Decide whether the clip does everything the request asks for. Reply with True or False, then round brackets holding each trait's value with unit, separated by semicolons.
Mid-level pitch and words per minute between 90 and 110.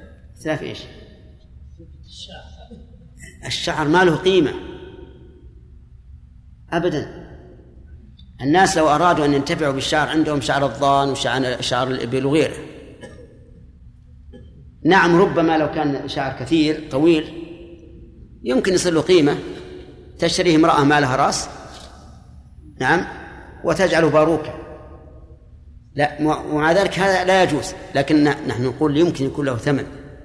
True (145 Hz; 100 wpm)